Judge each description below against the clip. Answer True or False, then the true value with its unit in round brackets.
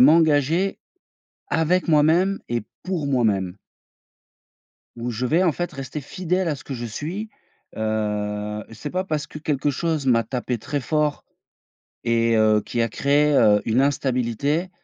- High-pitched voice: False (140 Hz)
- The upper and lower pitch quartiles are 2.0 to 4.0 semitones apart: False (5.4 semitones)